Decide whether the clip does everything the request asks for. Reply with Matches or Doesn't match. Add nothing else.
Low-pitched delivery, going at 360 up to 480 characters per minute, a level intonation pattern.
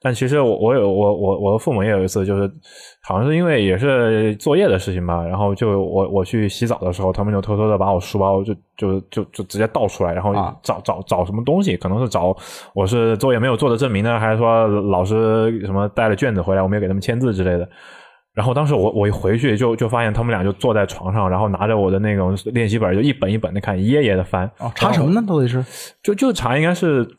Doesn't match